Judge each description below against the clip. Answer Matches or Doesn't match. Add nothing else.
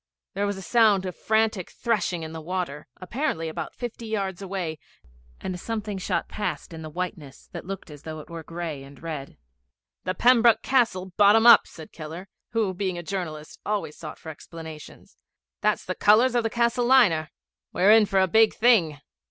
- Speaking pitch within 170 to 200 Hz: Matches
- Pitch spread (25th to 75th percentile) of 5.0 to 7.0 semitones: Matches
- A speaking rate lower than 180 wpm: Doesn't match